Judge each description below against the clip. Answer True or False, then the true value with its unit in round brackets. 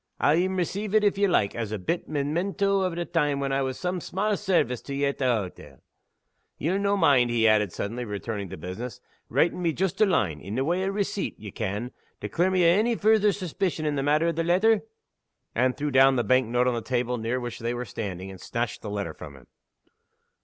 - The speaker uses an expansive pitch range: True (8.1 semitones)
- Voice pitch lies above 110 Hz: True (140 Hz)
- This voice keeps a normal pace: False (235 wpm)